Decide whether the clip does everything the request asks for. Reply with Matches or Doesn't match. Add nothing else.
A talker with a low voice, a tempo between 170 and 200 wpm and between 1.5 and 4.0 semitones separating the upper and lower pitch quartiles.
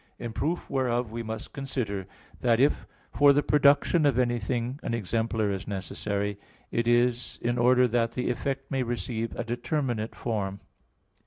Doesn't match